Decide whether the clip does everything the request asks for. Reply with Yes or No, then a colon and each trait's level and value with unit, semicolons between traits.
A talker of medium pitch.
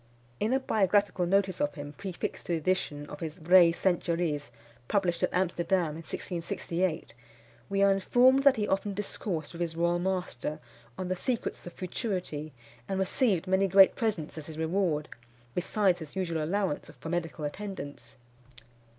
Yes: medium, 180 Hz